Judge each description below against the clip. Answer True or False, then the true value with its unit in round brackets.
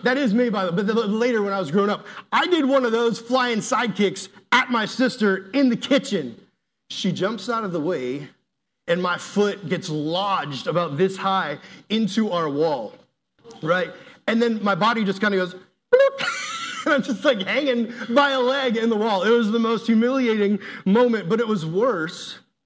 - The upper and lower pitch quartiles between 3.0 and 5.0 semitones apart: True (4.2 semitones)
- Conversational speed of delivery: True (195 wpm)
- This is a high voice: True (220 Hz)